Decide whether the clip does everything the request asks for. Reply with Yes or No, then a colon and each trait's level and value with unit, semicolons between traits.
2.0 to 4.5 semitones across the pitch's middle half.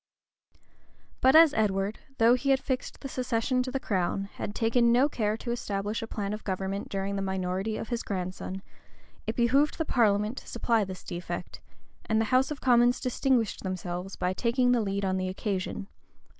Yes: average, 4.2 semitones